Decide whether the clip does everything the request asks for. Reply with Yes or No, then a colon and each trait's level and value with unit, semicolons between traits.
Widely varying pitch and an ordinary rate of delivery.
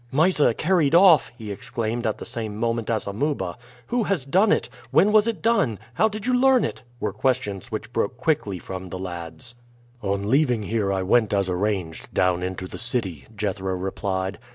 Yes: wide, 7.7 semitones; average, 185 wpm